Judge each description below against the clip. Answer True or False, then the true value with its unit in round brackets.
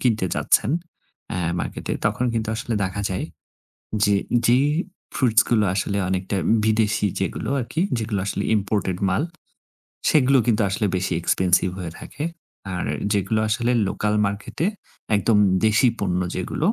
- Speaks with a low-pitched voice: True (105 Hz)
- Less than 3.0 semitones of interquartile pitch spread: False (3.4 semitones)